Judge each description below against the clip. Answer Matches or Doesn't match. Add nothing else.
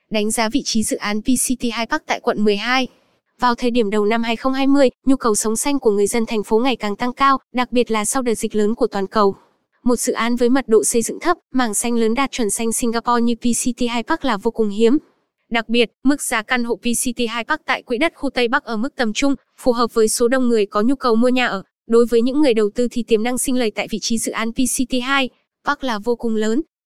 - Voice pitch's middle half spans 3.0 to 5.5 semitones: Doesn't match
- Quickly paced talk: Matches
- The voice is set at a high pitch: Matches